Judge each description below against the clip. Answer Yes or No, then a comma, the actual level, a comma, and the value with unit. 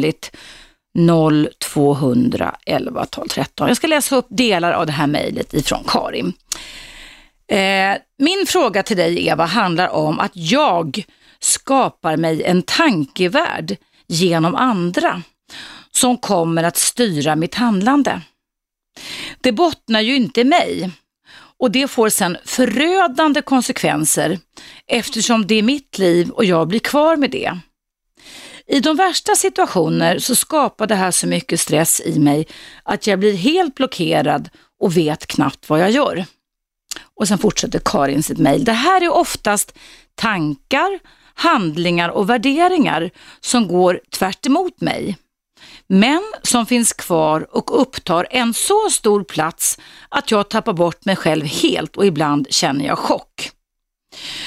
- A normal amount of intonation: No, wide, 7.9 semitones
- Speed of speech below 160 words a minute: Yes, average, 135 wpm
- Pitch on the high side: Yes, high, 210 Hz